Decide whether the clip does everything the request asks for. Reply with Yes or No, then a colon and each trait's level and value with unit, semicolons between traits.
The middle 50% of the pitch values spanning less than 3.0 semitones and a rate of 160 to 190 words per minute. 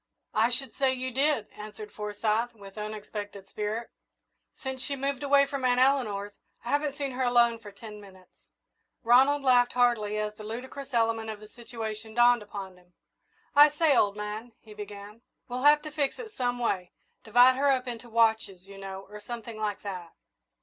No: average, 3.7 semitones; average, 180 wpm